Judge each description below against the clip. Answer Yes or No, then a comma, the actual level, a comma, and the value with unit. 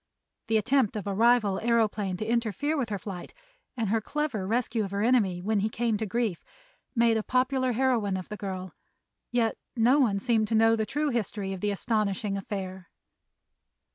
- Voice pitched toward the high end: Yes, high, 220 Hz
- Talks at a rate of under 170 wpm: No, average, 185 wpm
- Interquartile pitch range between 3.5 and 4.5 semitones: No, average, 3.1 semitones